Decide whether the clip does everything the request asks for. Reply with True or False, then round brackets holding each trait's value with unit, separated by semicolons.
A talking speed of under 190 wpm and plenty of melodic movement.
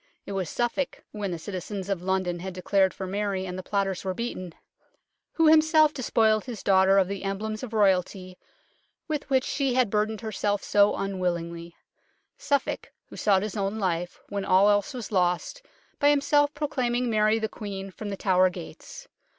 False (175 wpm; 3.9 semitones)